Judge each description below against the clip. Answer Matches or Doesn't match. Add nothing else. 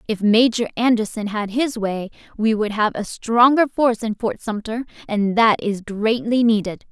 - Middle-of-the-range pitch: Doesn't match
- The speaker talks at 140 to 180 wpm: Matches